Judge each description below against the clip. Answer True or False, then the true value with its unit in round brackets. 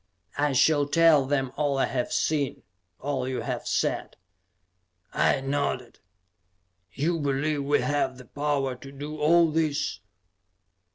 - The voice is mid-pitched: True (145 Hz)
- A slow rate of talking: True (130 wpm)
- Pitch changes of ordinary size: False (2.0 semitones)